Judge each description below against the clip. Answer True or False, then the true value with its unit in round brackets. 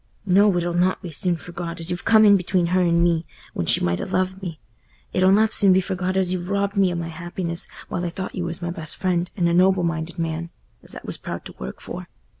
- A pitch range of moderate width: False (1.8 semitones)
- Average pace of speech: False (245 wpm)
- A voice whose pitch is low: False (175 Hz)